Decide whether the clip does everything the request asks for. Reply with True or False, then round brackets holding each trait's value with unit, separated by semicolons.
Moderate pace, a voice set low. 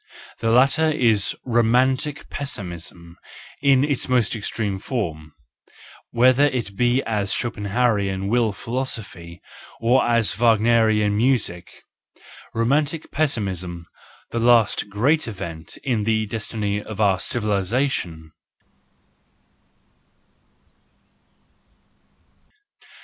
False (90 wpm; 115 Hz)